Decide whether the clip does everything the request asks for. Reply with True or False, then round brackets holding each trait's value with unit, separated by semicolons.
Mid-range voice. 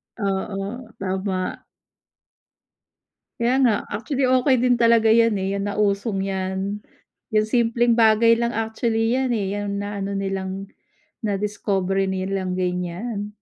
False (205 Hz)